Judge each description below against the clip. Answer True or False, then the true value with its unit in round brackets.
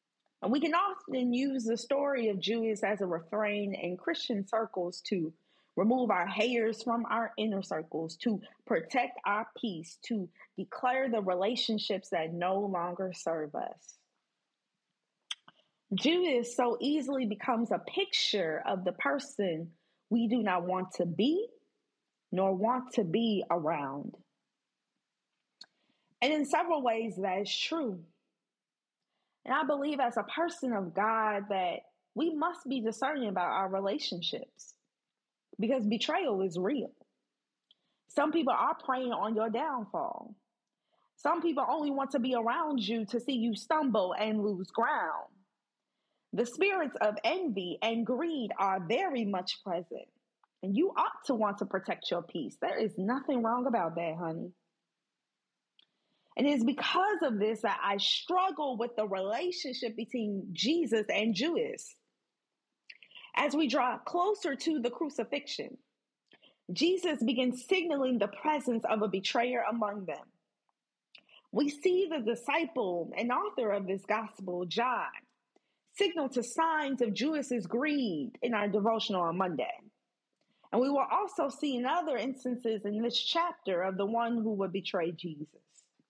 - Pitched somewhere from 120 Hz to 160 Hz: False (235 Hz)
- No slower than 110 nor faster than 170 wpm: True (140 wpm)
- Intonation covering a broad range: True (5.9 semitones)